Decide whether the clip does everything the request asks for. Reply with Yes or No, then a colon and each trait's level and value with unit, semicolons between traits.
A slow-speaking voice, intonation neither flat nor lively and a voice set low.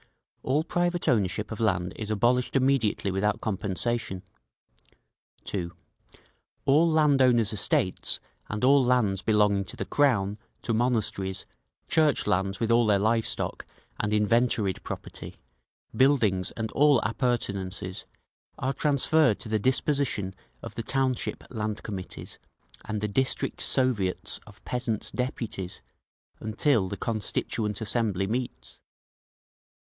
Yes: slow, 120 wpm; average, 4.3 semitones; low, 110 Hz